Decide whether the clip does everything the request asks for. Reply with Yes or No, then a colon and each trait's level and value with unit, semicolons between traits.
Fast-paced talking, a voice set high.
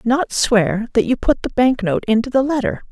Yes: fast, 225 wpm; high, 240 Hz